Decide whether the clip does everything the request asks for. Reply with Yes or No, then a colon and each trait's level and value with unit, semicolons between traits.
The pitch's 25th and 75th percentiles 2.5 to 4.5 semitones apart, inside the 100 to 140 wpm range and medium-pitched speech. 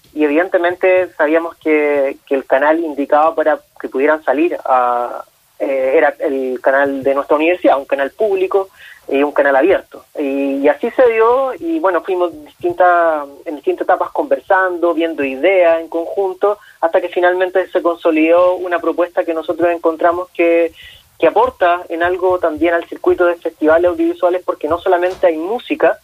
No: average, 2.8 semitones; average, 160 wpm; medium, 170 Hz